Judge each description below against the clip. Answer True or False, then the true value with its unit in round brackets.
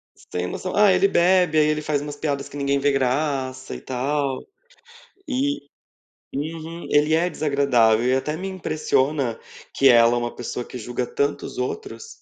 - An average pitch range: True (3.7 semitones)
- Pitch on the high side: False (145 Hz)